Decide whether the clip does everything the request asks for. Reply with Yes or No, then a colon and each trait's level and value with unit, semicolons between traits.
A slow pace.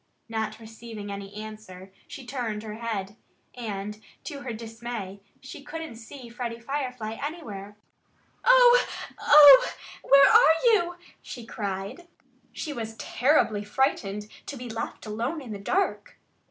Yes: slow, 130 wpm